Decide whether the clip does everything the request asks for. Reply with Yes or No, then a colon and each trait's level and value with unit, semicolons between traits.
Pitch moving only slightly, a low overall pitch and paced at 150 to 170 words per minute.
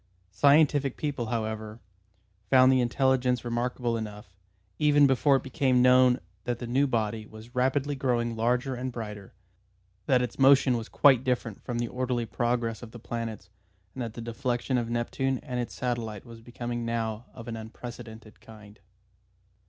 Yes: narrow, 2.1 semitones; low, 120 Hz; average, 160 wpm